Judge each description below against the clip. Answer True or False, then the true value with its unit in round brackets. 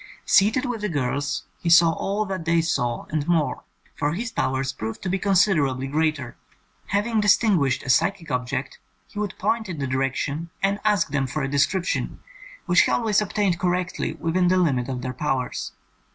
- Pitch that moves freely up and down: True (6.4 semitones)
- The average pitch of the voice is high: False (165 Hz)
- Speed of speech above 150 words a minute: True (180 wpm)